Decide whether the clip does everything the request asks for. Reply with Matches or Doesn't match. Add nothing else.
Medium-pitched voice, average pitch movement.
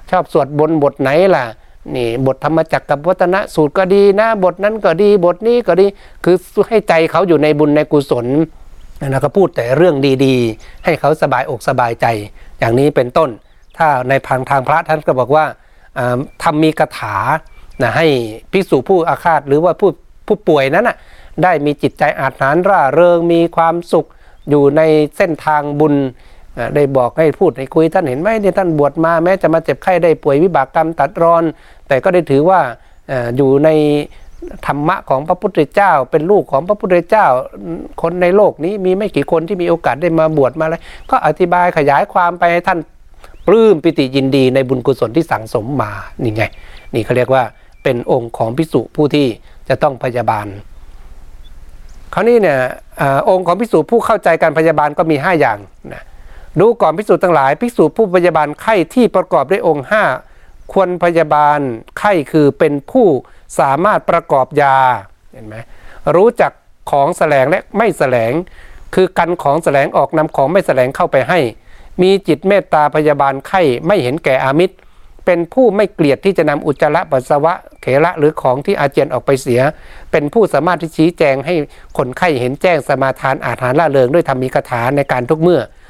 Matches